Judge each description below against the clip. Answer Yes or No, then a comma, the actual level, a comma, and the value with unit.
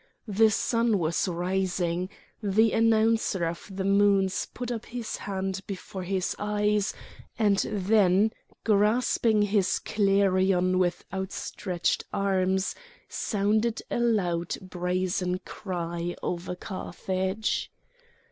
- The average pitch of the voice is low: No, high, 195 Hz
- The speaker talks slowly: Yes, slow, 100 wpm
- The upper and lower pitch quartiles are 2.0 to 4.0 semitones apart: Yes, narrow, 2.5 semitones